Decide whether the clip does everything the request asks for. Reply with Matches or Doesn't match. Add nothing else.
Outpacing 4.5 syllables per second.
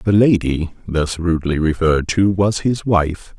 Doesn't match